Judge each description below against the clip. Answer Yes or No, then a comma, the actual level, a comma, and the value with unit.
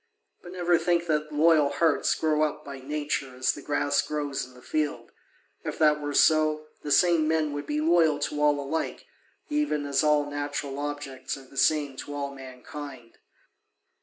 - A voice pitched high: No, medium, 145 Hz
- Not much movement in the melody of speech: Yes, narrow, 1.6 semitones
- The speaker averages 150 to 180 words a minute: Yes, average, 175 wpm